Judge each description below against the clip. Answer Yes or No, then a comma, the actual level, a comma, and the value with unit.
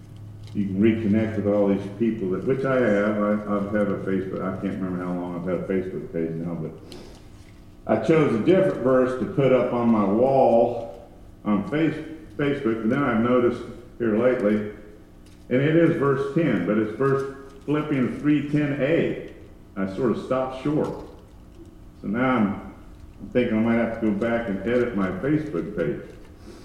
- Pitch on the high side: No, low, 115 Hz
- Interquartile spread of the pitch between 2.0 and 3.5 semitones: No, average, 4.4 semitones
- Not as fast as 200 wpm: Yes, average, 180 wpm